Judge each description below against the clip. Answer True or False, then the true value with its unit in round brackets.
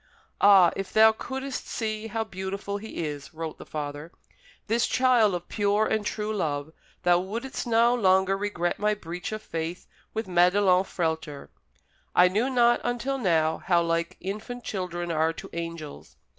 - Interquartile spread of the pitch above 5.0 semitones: False (4.6 semitones)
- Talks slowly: False (155 wpm)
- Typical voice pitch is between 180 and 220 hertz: True (190 Hz)